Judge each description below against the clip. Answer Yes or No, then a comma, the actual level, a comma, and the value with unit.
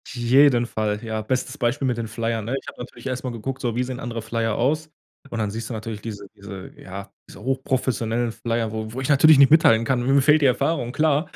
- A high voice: No, low, 120 Hz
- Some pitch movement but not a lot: Yes, average, 3.0 semitones